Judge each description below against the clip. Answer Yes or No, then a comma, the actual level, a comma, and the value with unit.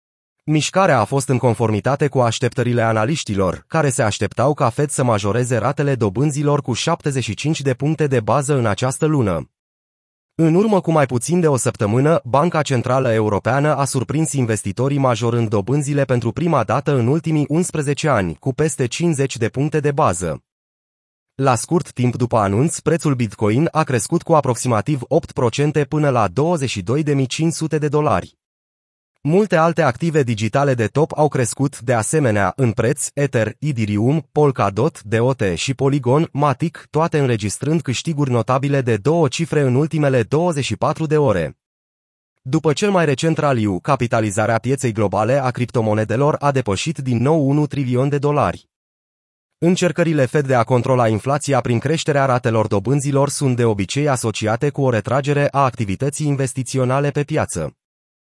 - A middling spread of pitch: Yes, average, 4.2 semitones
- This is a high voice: No, low, 135 Hz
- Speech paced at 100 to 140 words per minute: No, average, 150 wpm